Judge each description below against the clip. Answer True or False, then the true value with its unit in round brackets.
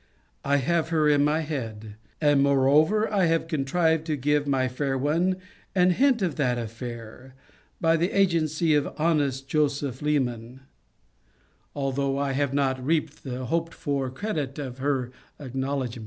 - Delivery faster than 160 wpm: False (145 wpm)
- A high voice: False (145 Hz)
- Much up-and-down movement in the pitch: False (3.4 semitones)